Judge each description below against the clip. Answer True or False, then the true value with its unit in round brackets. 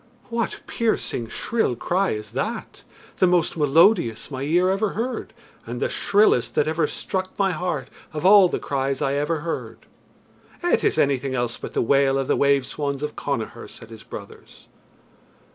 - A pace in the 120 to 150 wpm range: False (170 wpm)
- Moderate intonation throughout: False (5.8 semitones)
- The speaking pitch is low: False (150 Hz)